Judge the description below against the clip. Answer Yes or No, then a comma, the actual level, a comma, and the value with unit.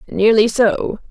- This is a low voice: No, high, 220 Hz